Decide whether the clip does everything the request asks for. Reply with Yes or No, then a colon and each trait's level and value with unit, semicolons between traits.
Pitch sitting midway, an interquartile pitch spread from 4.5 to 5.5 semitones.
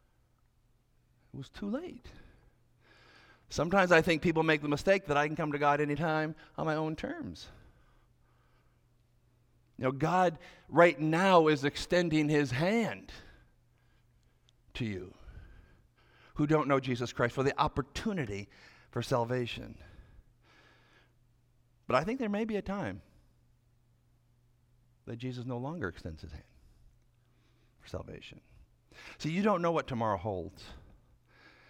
No: low, 125 Hz; average, 4.8 semitones